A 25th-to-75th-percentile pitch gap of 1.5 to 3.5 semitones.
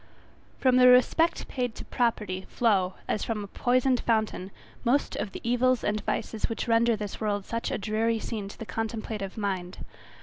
Yes: average, 2.8 semitones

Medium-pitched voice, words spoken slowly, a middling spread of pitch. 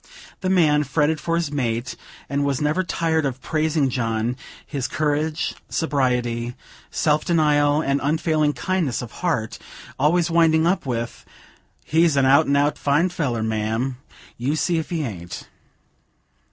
No: medium, 145 Hz; average, 145 wpm; average, 3.9 semitones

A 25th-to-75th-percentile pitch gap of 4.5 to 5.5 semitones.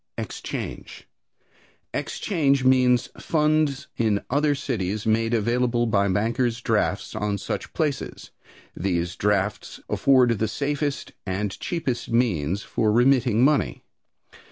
Yes: average, 4.9 semitones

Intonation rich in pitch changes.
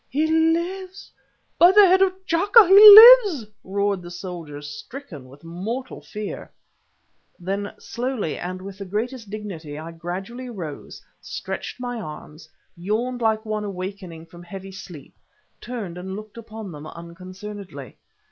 Yes: wide, 6.3 semitones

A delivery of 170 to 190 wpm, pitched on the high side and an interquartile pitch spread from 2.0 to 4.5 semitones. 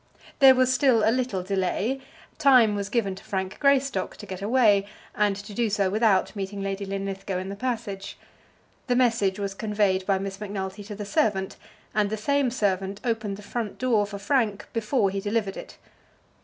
Yes: average, 185 wpm; high, 205 Hz; average, 3.0 semitones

